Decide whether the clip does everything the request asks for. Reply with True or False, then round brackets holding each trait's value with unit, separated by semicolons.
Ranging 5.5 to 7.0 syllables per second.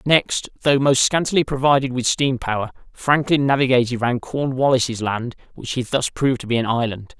False (5.2 syllables/s)